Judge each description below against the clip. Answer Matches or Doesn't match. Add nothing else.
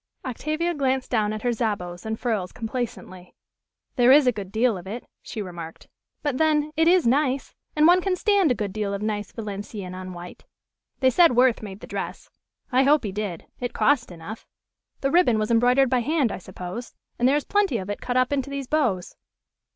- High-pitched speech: Matches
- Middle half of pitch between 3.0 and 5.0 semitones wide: Doesn't match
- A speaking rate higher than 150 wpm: Matches